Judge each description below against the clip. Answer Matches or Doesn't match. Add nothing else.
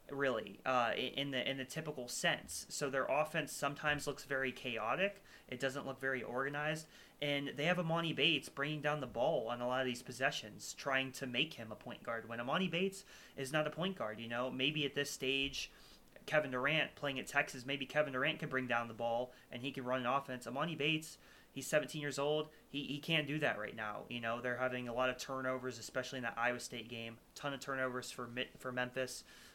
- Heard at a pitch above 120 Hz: Matches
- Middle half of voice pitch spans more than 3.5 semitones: Doesn't match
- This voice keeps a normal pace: Doesn't match